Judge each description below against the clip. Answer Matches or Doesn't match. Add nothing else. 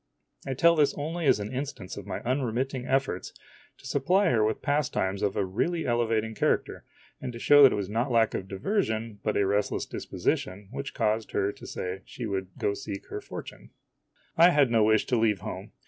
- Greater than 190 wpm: Matches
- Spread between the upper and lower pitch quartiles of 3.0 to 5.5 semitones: Matches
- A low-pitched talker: Matches